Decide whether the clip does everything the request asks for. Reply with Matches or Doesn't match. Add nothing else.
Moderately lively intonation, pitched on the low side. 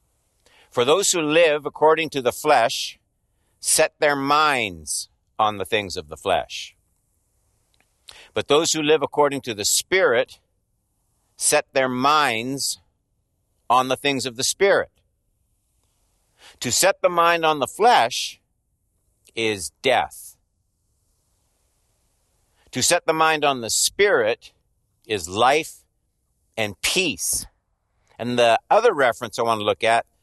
Doesn't match